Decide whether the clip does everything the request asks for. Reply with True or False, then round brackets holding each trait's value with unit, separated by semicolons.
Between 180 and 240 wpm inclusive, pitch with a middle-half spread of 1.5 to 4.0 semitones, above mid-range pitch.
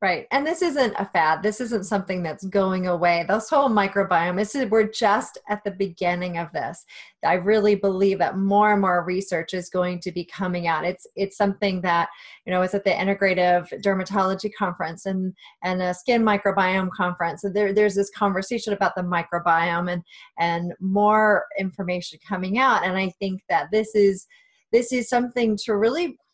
True (185 wpm; 2.7 semitones; 195 Hz)